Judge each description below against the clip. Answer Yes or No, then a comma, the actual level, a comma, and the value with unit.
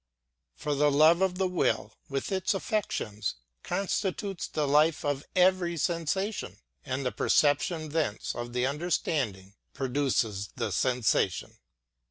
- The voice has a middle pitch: Yes, medium, 150 Hz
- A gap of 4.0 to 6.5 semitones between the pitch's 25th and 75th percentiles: Yes, wide, 5.4 semitones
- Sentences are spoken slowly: Yes, slow, 130 wpm